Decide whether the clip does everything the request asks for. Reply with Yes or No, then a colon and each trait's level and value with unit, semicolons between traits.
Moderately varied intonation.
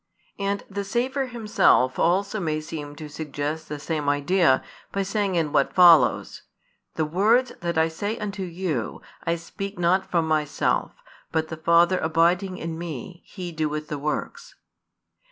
Yes: average, 4.0 semitones